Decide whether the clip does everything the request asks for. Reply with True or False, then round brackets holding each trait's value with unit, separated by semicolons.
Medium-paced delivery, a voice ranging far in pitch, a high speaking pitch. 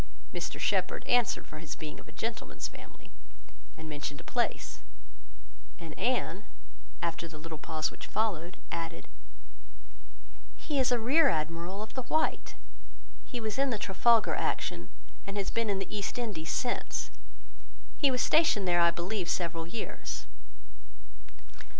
True (145 wpm; 5.8 semitones; 195 Hz)